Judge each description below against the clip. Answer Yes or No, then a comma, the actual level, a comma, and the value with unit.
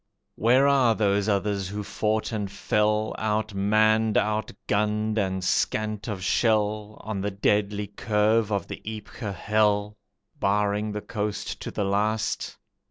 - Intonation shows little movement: Yes, narrow, 1.0 semitones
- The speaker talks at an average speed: No, slow, 130 wpm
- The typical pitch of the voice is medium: No, low, 105 Hz